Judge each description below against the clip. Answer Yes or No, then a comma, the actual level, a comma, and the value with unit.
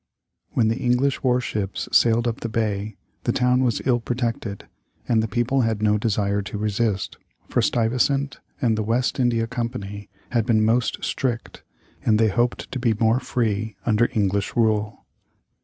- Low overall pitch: Yes, low, 115 Hz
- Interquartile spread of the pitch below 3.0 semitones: Yes, narrow, 2.4 semitones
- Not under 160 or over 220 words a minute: Yes, average, 170 wpm